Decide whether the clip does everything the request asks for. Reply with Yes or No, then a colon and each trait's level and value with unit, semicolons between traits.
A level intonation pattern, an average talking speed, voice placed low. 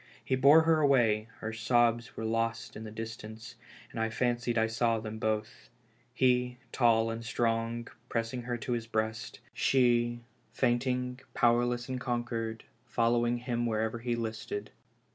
Yes: narrow, 1.4 semitones; average, 150 wpm; low, 120 Hz